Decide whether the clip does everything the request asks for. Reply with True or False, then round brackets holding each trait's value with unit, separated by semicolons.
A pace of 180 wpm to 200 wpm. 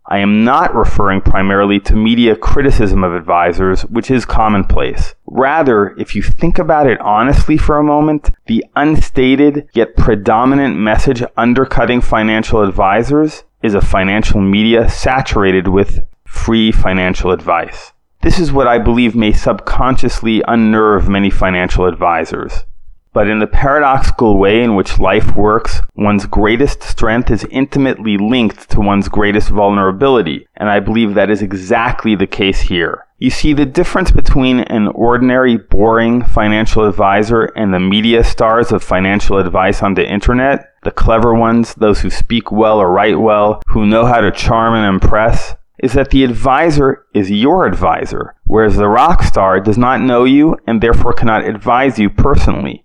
False (155 wpm)